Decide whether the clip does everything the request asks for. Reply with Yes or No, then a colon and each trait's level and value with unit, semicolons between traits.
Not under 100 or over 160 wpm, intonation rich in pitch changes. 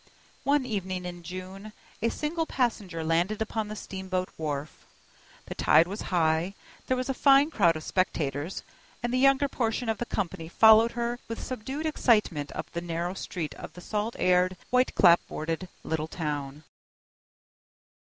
Yes: average, 155 wpm; wide, 6.0 semitones